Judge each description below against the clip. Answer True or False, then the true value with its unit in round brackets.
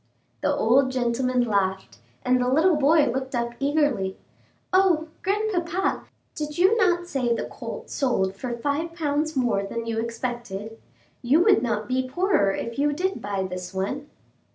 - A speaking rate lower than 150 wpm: False (155 wpm)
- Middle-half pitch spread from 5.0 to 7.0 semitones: True (5.5 semitones)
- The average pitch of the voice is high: True (260 Hz)